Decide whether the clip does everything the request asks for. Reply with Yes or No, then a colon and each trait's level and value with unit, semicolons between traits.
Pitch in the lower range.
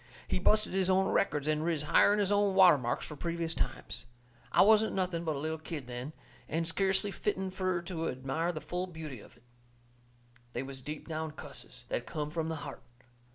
No: medium, 165 Hz